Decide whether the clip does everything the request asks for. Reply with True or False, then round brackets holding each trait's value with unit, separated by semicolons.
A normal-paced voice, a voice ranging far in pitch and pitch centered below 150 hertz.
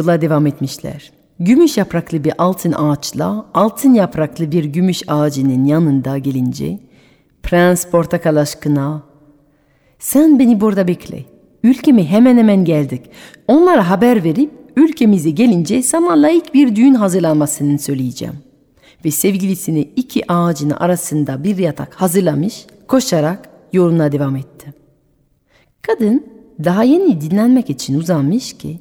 False (115 wpm; 7.1 semitones; 175 Hz)